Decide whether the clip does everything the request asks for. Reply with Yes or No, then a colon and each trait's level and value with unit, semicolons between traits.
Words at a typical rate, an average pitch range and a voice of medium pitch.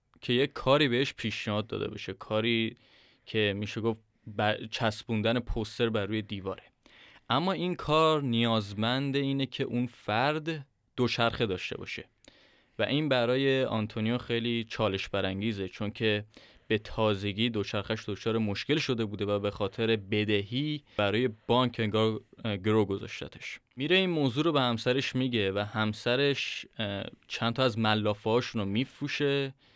No: average, 135 wpm; average, 3.4 semitones; low, 115 Hz